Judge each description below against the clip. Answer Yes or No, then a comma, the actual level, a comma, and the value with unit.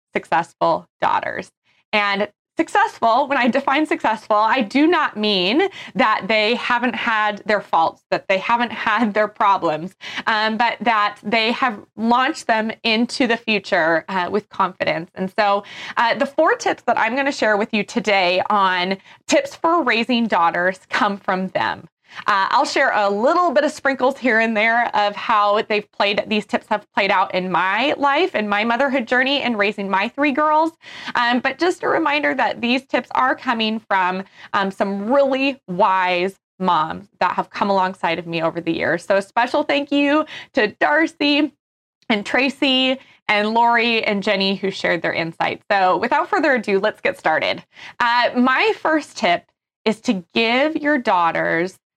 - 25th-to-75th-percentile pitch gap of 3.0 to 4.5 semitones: No, wide, 5.4 semitones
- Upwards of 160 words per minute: Yes, average, 170 wpm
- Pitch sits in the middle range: No, high, 230 Hz